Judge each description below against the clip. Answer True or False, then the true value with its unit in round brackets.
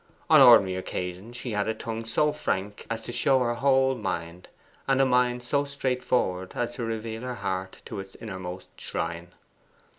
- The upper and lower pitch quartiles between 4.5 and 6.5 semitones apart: True (5.0 semitones)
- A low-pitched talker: True (115 Hz)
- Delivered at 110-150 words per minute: False (175 wpm)